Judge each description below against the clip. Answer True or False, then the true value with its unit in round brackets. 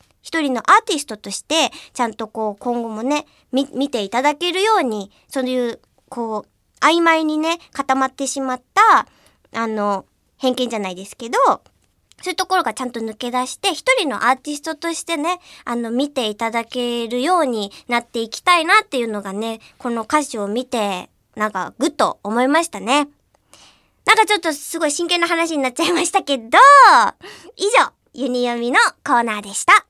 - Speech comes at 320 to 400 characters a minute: True (355 characters per minute)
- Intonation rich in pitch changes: True (6.1 semitones)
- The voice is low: False (255 Hz)